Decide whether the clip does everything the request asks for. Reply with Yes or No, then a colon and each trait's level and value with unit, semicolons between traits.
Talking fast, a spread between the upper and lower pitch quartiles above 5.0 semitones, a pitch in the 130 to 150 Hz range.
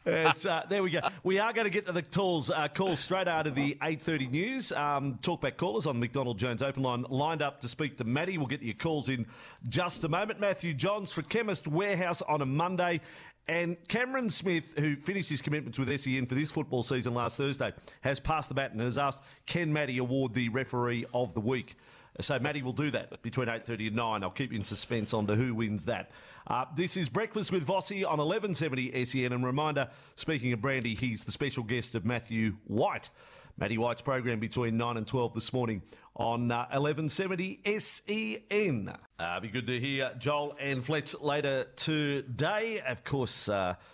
Yes: fast, 210 wpm; wide, 5.6 semitones; medium, 140 Hz